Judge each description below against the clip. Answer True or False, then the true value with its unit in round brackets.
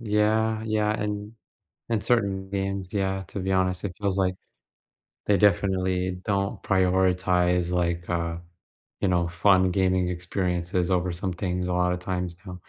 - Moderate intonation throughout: False (1.7 semitones)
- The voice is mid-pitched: False (95 Hz)